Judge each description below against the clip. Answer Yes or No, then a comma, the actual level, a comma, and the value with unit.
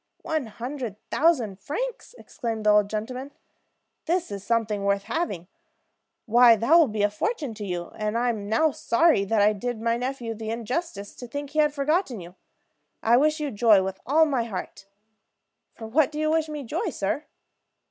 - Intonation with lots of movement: Yes, wide, 6.0 semitones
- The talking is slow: No, average, 185 wpm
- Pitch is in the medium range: No, high, 235 Hz